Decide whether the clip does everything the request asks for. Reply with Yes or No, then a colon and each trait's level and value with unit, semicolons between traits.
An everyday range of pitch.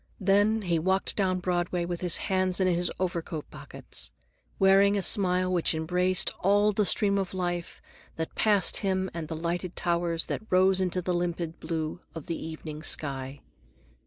No: narrow, 2.1 semitones